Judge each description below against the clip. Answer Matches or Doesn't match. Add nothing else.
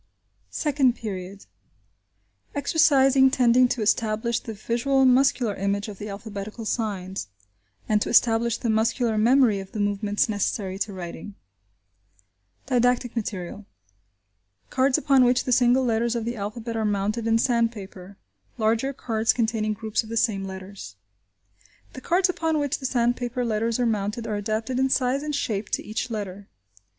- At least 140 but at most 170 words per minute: Matches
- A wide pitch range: Doesn't match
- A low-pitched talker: Doesn't match